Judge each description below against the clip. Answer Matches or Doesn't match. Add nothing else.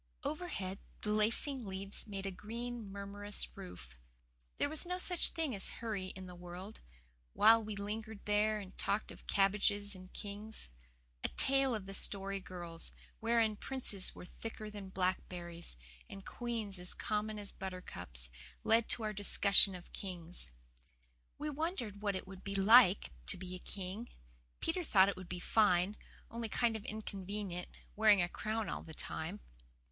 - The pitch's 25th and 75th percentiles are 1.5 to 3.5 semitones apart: Matches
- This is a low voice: Doesn't match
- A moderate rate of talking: Matches